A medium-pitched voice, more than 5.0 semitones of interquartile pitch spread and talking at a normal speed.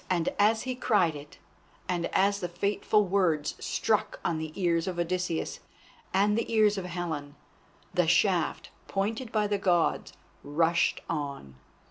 No: medium, 180 Hz; average, 3.8 semitones; average, 145 wpm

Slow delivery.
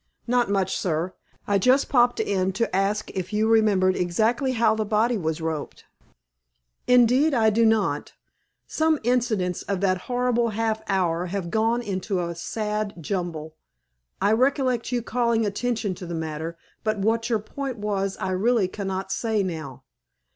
No: average, 155 wpm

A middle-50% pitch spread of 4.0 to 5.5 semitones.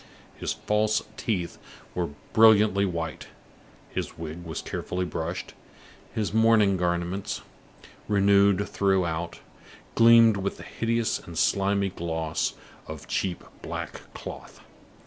No: average, 3.5 semitones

